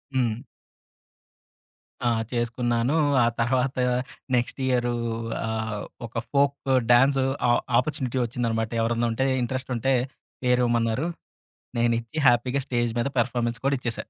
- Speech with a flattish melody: Yes, narrow, 2.0 semitones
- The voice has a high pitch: No, low, 120 Hz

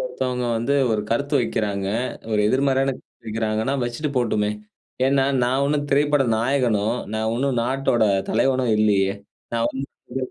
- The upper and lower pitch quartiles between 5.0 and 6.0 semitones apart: No, average, 3.7 semitones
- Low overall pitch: Yes, low, 125 Hz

